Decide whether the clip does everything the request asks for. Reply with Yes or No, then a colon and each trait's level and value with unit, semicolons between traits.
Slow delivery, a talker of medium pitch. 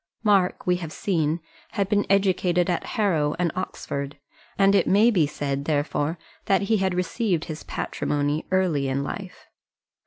No: average, 155 wpm; medium, 180 Hz